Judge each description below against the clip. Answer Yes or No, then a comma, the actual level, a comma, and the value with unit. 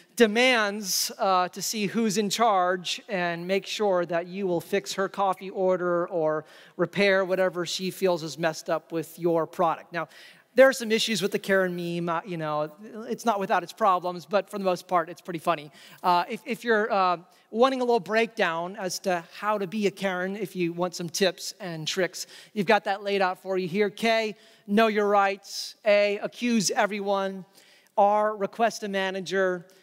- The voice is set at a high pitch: Yes, high, 195 Hz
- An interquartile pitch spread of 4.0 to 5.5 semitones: No, average, 2.8 semitones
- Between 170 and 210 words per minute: Yes, average, 190 wpm